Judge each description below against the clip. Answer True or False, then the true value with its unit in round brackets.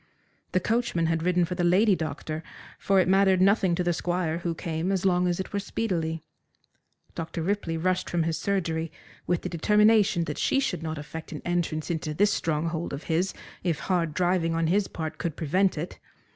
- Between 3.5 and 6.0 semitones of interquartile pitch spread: False (2.6 semitones)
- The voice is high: False (175 Hz)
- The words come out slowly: False (195 wpm)